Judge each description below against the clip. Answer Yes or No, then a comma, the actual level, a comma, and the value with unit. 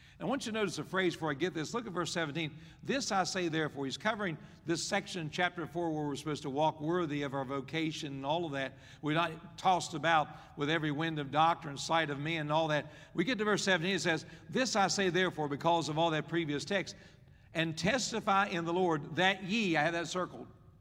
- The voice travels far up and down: No, average, 3.2 semitones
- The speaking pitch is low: No, medium, 165 Hz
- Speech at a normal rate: No, fast, 235 wpm